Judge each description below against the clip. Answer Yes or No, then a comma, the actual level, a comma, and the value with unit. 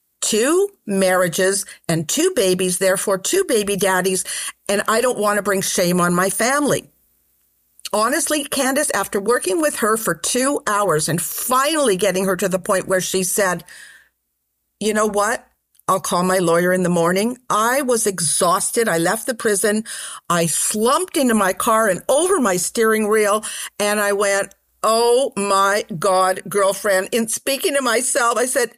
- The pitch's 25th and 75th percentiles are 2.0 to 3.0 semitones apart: No, average, 3.9 semitones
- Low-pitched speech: No, high, 205 Hz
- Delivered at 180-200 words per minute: No, average, 165 wpm